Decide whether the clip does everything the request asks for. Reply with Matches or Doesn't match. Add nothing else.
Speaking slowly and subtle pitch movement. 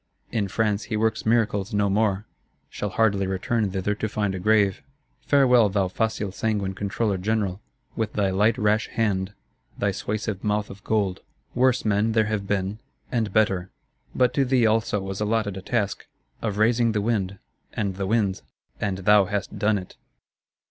Doesn't match